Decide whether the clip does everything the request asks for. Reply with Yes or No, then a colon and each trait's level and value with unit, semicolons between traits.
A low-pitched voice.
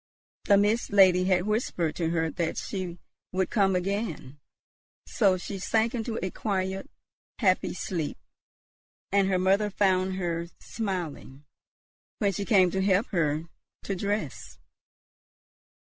No: high, 190 Hz